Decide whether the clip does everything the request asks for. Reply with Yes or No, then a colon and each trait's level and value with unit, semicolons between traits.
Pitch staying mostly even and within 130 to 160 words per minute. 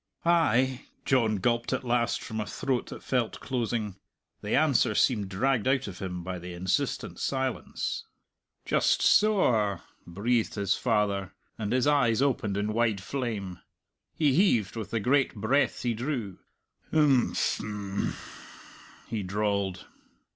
No: average, 4.4 semitones; average, 140 wpm